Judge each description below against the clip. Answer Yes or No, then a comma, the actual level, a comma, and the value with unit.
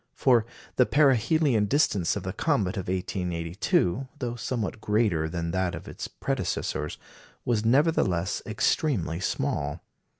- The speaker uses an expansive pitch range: Yes, wide, 5.9 semitones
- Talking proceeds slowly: Yes, slow, 125 wpm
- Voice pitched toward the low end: Yes, low, 105 Hz